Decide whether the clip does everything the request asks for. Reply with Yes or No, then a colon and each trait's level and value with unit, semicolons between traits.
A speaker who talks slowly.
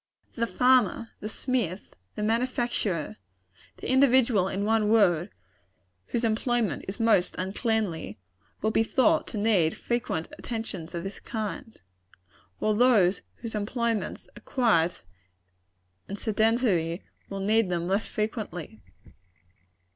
Yes: slow, 115 wpm